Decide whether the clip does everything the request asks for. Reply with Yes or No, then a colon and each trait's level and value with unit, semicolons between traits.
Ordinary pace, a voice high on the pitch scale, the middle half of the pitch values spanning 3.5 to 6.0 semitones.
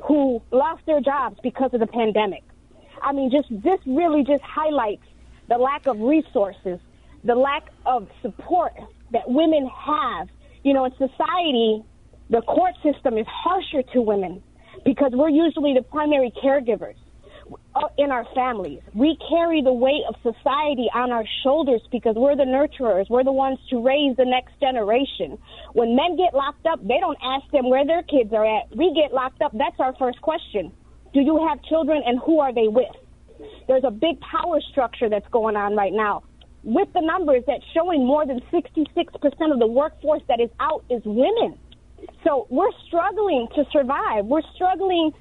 Yes: average, 175 wpm; very high, 275 Hz; average, 3.9 semitones